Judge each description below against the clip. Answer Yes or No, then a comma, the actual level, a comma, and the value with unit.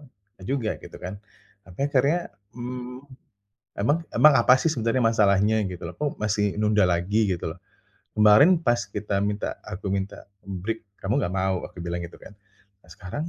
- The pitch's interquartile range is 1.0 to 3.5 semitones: No, average, 3.9 semitones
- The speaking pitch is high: No, low, 105 Hz